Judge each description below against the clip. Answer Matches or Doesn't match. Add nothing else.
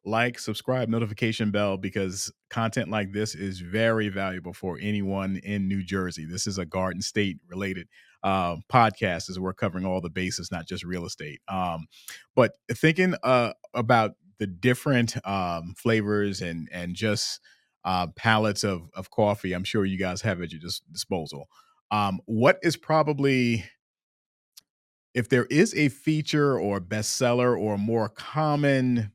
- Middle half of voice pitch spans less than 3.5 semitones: Doesn't match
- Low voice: Matches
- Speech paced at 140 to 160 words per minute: Matches